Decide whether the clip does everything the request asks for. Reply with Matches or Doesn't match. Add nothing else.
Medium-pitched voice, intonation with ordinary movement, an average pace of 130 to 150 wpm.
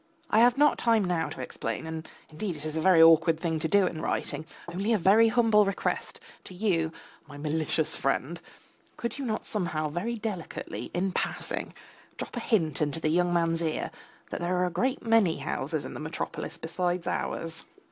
Doesn't match